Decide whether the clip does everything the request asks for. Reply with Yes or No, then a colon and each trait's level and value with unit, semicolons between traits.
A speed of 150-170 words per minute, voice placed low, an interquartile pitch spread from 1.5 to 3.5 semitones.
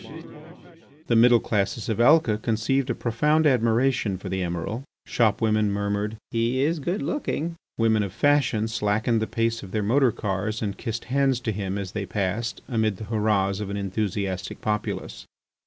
Yes: average, 165 wpm; low, 110 Hz; average, 2.9 semitones